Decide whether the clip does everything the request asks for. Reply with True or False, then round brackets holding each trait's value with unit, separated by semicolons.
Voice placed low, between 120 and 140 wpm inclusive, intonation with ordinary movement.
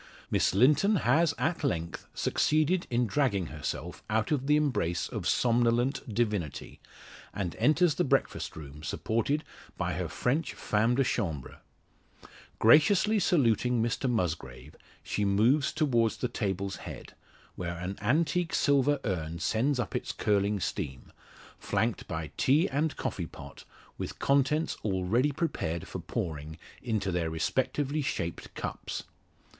False (115 Hz; 135 wpm; 8.1 semitones)